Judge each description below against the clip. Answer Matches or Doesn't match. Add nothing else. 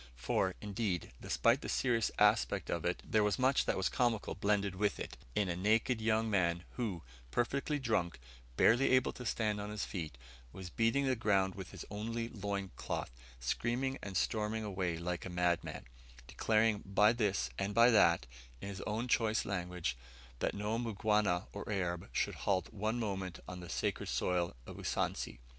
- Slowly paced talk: Doesn't match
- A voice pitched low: Matches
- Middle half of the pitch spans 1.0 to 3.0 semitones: Doesn't match